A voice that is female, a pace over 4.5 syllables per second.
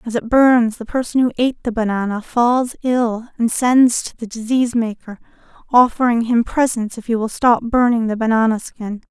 Yes: female; 5.0 syllables/s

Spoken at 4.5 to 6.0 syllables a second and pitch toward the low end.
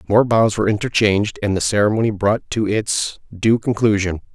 Yes: 5.4 syllables/s; low, 105 Hz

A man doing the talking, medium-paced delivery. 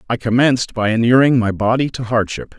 Yes: male; average, 185 wpm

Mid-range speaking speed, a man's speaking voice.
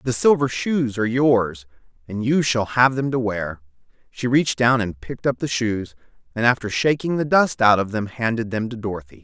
No: fast, 215 wpm; male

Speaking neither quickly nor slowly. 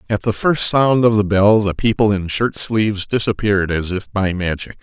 No: fast, 210 wpm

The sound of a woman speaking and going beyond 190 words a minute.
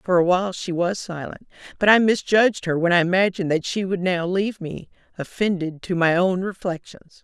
Yes: female; average, 200 wpm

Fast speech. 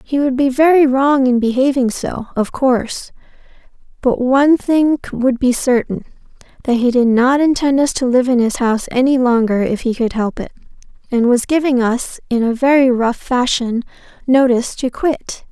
No: average, 175 wpm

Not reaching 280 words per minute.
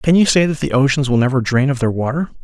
No: fast, 295 wpm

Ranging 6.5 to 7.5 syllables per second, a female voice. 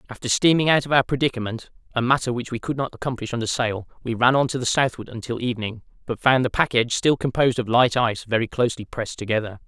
No: 6.7 syllables/s; male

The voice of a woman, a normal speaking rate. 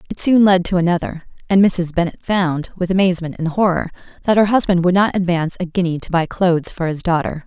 No: female; fast, 215 wpm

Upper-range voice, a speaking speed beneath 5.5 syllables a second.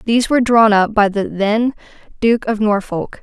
Yes: high, 215 Hz; 4.9 syllables/s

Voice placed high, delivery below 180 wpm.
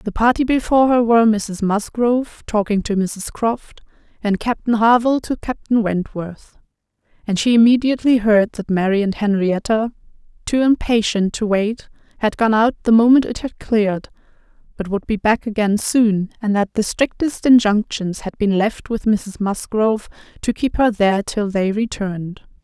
Yes: high, 220 Hz; average, 160 wpm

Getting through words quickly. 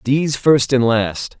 No: average, 170 wpm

